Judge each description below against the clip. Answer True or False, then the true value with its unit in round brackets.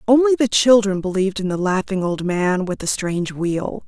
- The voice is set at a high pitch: True (200 Hz)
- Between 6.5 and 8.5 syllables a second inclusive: False (5.1 syllables/s)